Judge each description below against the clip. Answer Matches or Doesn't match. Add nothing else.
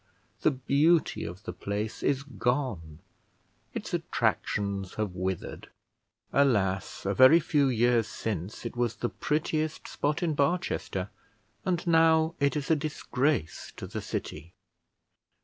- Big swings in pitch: Matches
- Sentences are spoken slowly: Matches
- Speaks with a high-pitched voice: Doesn't match